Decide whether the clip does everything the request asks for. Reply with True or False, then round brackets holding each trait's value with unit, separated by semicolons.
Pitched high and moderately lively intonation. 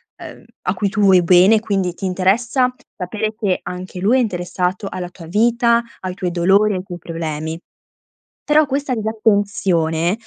True (195 Hz; 3.5 semitones)